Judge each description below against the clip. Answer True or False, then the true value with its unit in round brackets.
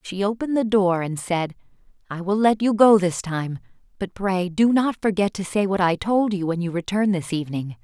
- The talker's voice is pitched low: False (190 Hz)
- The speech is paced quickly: True (220 wpm)